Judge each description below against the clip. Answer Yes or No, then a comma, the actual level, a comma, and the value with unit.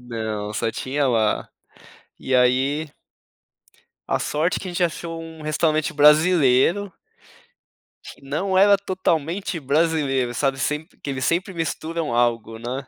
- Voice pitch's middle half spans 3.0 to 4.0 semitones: No, average, 4.6 semitones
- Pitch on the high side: No, medium, 150 Hz